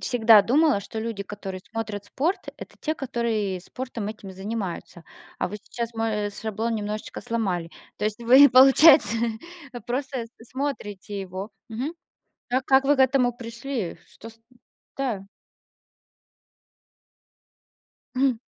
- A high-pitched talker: Yes, high, 230 Hz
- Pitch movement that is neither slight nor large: Yes, average, 3.9 semitones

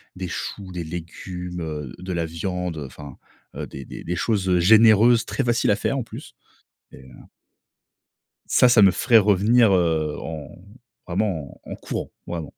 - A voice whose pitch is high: No, very low, 90 Hz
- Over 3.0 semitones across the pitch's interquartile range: Yes, average, 4.5 semitones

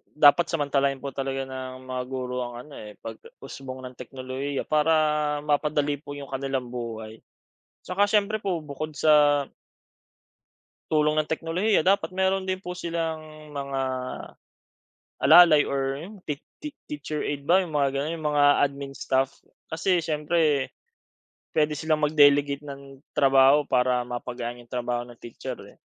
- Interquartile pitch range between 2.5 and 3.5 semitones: Yes, average, 2.9 semitones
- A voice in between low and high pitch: Yes, medium, 145 Hz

